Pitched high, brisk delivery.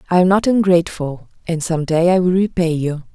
No: medium, 175 Hz; fast, 210 wpm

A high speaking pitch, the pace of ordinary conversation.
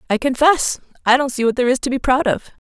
No: very high, 260 Hz; fast, 270 wpm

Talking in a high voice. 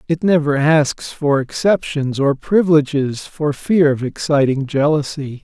No: medium, 145 Hz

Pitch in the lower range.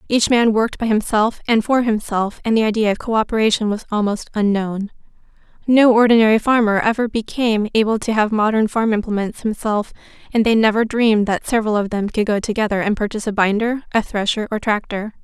No: high, 215 Hz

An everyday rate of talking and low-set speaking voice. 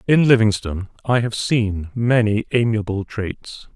No: slow, 130 wpm; low, 110 Hz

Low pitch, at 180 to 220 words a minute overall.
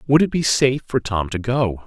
No: low, 125 Hz; fast, 255 wpm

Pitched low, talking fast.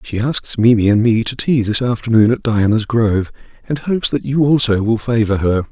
Yes: low, 115 Hz; fast, 210 wpm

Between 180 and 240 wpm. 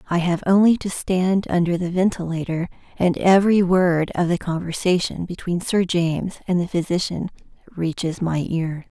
No: average, 155 wpm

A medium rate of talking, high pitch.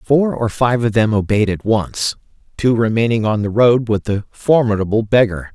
No: average, 185 wpm; low, 110 Hz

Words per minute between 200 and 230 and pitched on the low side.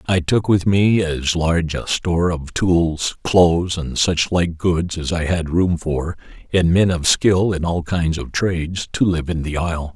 Yes: fast, 205 wpm; very low, 85 Hz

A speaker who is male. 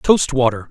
Yes: male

